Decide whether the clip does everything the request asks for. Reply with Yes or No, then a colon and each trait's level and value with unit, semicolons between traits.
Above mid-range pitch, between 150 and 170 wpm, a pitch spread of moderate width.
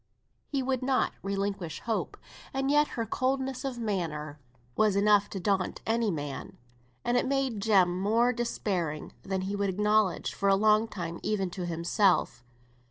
Yes: high, 205 Hz; average, 160 wpm; average, 4.3 semitones